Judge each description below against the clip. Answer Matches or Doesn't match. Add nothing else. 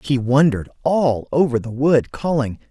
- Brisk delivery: Doesn't match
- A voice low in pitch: Matches